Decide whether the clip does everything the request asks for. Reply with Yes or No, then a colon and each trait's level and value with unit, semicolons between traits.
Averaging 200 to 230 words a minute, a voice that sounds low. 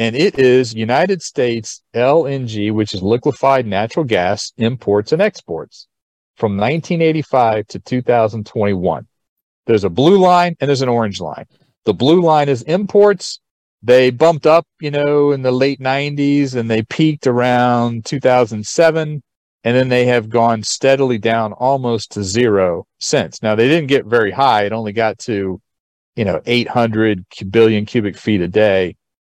No: average, 155 wpm; low, 120 Hz